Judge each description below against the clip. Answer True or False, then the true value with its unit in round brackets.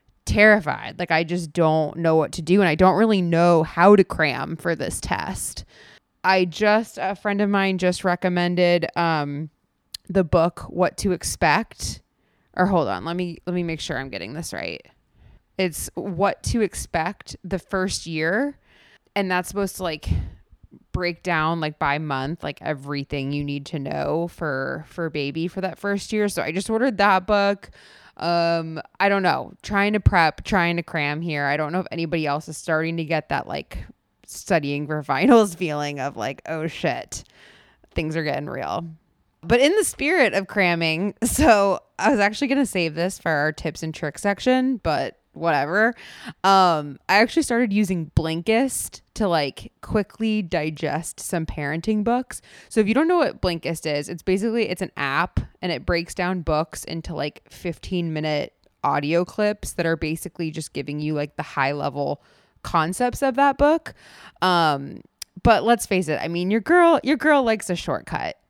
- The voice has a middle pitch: True (175 Hz)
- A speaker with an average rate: True (180 wpm)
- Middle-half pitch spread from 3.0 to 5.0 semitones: True (4.2 semitones)